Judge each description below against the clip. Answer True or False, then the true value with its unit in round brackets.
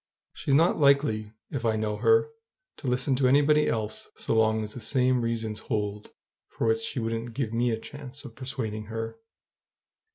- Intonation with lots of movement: False (3.7 semitones)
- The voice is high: False (115 Hz)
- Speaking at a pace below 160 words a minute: False (175 wpm)